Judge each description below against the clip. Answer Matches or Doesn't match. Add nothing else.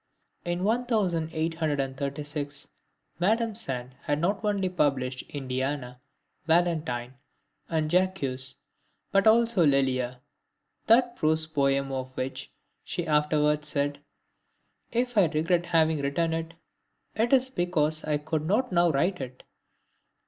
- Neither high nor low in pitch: Matches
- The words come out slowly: Matches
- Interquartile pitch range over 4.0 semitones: Matches